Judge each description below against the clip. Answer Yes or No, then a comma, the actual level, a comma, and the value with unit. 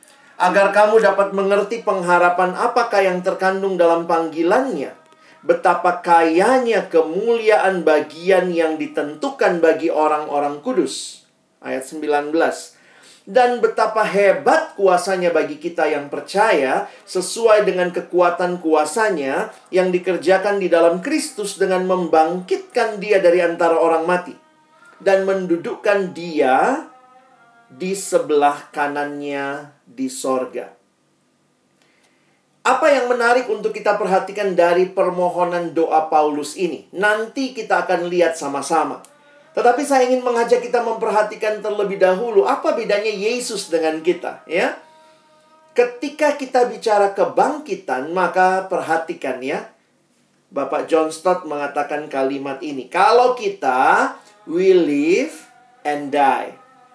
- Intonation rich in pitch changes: Yes, wide, 6.1 semitones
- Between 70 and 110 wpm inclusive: Yes, average, 105 wpm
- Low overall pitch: No, high, 190 Hz